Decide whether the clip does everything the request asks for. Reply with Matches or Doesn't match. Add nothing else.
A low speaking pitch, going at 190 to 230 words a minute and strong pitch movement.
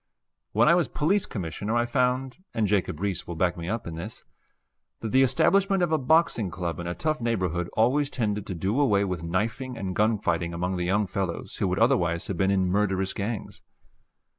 Matches